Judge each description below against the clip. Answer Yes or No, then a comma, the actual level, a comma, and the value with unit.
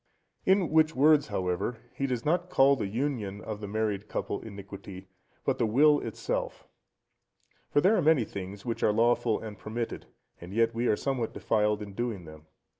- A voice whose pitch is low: Yes, low, 115 Hz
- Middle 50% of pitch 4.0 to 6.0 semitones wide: Yes, average, 5.1 semitones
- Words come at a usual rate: Yes, average, 180 wpm